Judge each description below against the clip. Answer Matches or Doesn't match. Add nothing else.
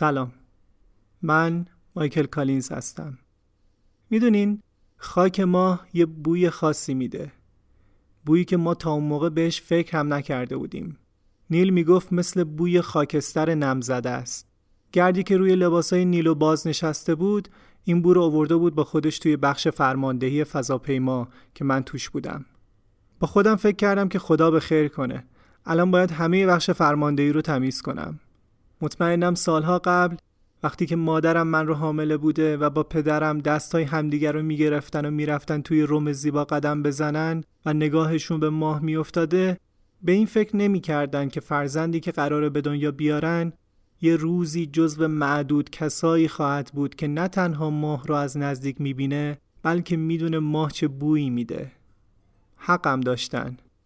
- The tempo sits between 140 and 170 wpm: Matches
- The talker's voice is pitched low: Doesn't match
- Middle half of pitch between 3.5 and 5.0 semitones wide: Doesn't match